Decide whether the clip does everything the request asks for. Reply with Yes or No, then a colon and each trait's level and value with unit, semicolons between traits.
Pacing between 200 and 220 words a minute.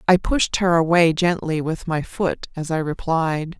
No: average, 185 wpm